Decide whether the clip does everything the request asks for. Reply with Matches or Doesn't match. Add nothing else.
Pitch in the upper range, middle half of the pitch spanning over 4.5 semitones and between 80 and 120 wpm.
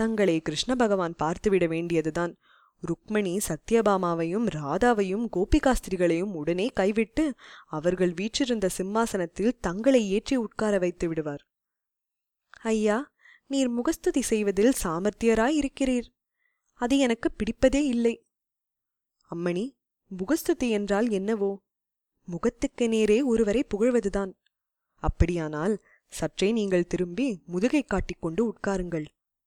Matches